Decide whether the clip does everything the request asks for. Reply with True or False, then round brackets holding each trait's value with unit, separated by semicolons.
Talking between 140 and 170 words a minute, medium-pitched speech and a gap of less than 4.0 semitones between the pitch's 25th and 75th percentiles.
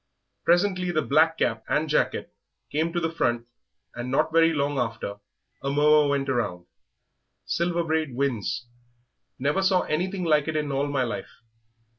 True (155 wpm; 150 Hz; 3.4 semitones)